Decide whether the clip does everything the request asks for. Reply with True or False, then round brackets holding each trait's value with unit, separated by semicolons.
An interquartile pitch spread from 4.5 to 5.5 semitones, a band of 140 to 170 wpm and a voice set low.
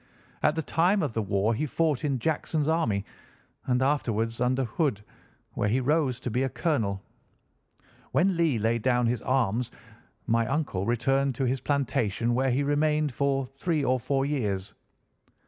False (4.1 semitones; 165 wpm; 130 Hz)